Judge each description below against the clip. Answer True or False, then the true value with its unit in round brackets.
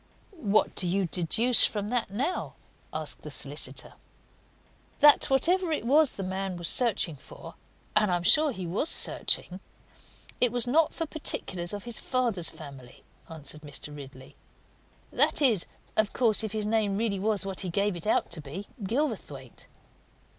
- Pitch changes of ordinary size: False (6.0 semitones)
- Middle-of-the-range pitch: False (205 Hz)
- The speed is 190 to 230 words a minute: False (165 wpm)